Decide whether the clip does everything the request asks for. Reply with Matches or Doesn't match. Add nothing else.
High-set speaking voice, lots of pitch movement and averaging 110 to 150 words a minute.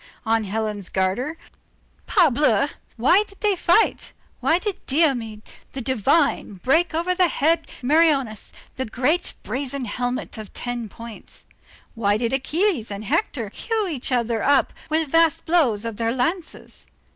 Matches